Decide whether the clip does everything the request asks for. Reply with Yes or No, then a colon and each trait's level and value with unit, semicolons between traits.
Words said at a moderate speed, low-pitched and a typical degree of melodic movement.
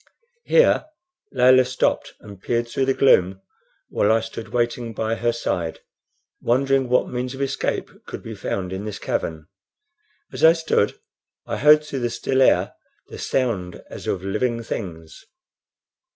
Yes: average, 150 wpm; low, 120 Hz; average, 4.5 semitones